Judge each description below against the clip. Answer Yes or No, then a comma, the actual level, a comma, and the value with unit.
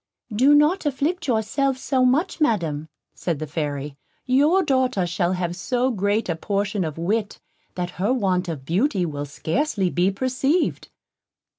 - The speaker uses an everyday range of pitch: No, wide, 7.4 semitones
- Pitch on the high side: Yes, high, 205 Hz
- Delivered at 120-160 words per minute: Yes, average, 150 wpm